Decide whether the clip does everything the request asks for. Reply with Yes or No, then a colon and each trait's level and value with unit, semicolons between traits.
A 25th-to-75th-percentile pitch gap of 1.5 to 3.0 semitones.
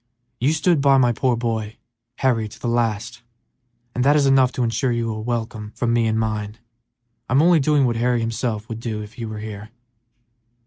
Yes: average, 2.7 semitones